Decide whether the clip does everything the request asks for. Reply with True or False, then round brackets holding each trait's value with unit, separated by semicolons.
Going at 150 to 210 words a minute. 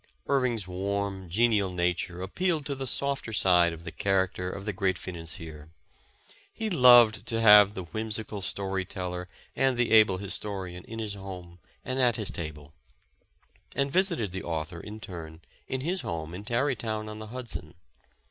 True (165 wpm)